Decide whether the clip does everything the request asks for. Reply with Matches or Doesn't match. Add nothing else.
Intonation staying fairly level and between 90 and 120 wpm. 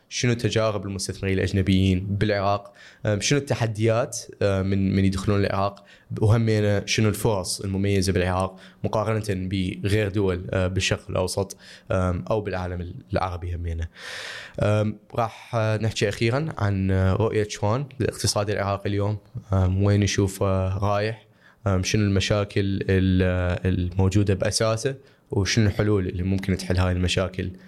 Matches